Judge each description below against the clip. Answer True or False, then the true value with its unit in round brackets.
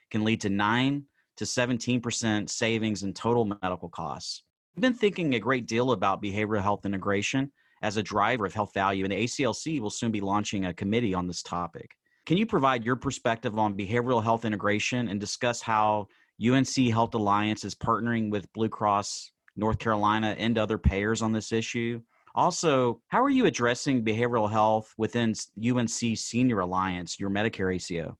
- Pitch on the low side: True (110 Hz)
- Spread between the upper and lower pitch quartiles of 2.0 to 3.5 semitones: True (2.9 semitones)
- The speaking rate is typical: True (170 wpm)